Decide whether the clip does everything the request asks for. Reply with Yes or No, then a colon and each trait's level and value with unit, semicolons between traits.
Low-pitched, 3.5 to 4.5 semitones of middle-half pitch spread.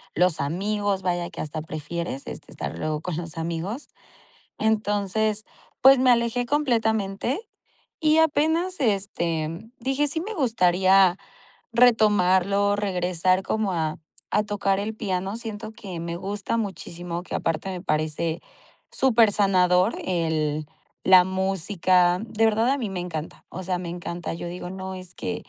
No: high, 190 Hz; average, 4.0 semitones